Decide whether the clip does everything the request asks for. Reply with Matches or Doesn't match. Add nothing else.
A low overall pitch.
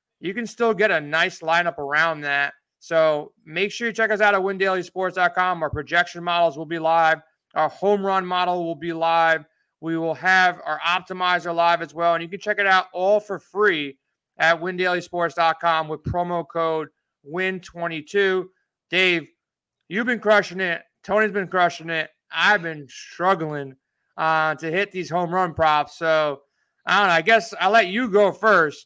Doesn't match